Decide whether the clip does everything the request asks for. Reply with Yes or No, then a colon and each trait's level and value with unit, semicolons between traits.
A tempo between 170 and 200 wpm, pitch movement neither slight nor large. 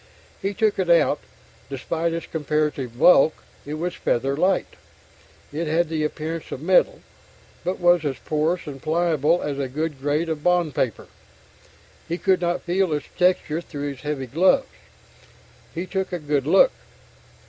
No: average, 160 wpm; average, 3.1 semitones